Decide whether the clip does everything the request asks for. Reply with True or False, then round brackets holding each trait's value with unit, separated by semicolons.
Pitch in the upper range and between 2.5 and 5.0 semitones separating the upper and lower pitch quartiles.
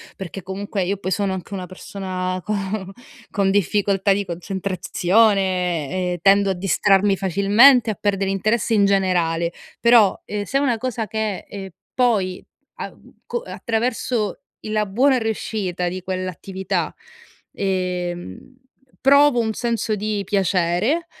True (195 Hz; 2.8 semitones)